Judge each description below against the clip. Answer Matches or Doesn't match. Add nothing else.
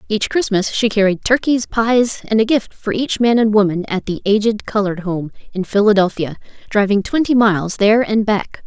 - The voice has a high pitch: Matches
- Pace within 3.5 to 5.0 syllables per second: Doesn't match